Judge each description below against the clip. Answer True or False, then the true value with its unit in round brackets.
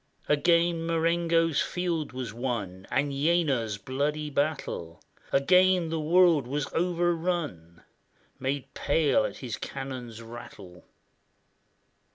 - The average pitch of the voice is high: False (145 Hz)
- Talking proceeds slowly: True (100 wpm)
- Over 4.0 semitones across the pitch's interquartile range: True (5.3 semitones)